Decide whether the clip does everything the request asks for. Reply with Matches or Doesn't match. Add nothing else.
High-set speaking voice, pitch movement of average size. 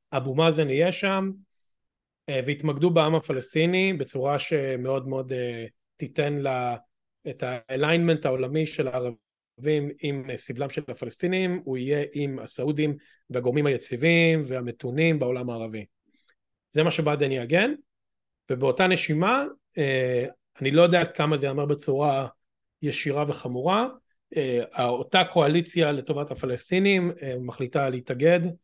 Doesn't match